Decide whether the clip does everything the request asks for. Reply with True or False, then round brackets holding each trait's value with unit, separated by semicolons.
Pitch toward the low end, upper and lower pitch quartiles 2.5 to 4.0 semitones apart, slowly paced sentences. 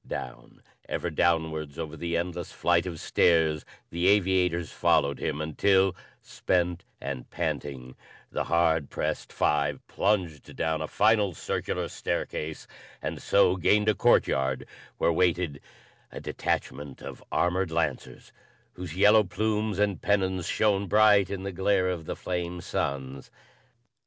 True (85 Hz; 3.5 semitones; 130 wpm)